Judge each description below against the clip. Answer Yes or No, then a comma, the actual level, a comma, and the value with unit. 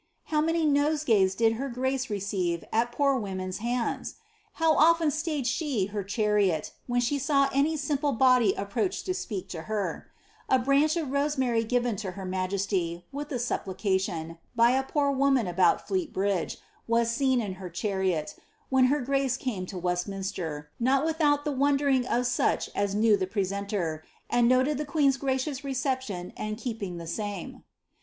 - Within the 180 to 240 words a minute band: No, average, 165 wpm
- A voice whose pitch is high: Yes, high, 240 Hz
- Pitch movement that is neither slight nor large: No, wide, 6.1 semitones